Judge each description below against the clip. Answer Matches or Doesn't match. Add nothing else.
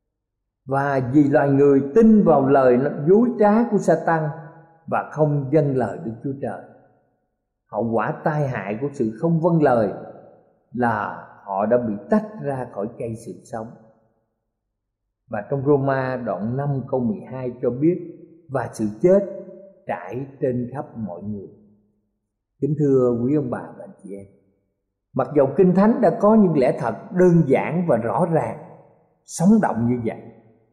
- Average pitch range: Doesn't match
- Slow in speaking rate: Matches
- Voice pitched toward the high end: Doesn't match